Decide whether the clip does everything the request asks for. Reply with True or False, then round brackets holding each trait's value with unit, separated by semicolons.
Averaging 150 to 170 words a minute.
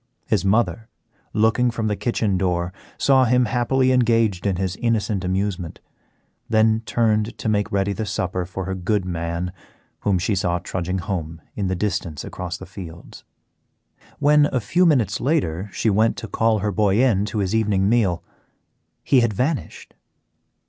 True (160 wpm)